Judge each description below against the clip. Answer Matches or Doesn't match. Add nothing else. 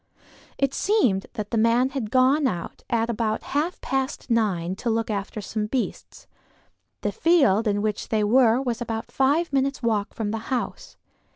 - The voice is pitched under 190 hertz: Doesn't match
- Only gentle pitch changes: Doesn't match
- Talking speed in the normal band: Matches